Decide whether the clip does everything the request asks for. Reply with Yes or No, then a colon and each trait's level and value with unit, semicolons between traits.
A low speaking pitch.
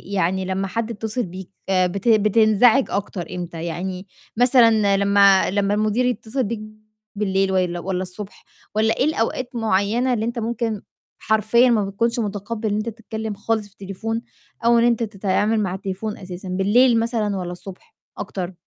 No: high, 210 Hz